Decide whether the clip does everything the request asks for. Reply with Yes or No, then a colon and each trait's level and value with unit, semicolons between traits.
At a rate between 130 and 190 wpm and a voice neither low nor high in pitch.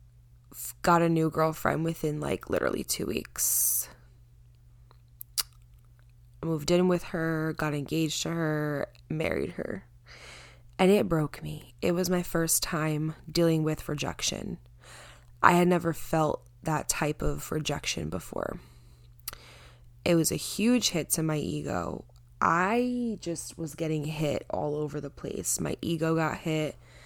Yes: slow, 135 wpm; medium, 155 Hz